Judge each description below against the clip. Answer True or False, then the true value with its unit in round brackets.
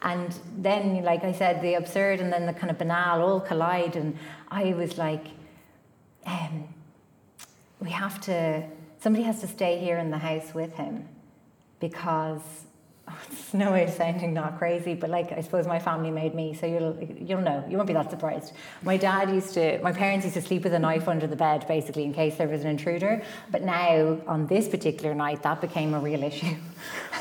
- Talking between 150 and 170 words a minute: False (205 wpm)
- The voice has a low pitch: False (170 Hz)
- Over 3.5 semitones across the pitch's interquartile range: False (2.5 semitones)